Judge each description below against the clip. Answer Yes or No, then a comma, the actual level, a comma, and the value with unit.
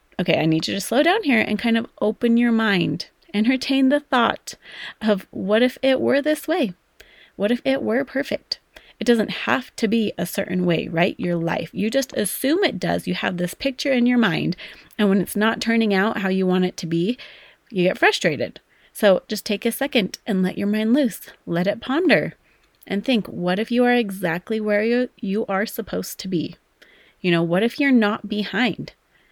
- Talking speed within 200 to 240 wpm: Yes, fast, 205 wpm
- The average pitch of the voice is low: No, high, 220 Hz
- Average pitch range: Yes, average, 4.8 semitones